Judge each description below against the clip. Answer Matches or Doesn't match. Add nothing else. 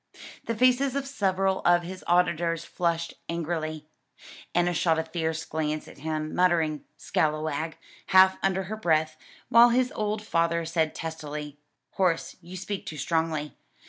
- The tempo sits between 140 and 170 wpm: Matches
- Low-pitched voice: Doesn't match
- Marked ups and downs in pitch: Doesn't match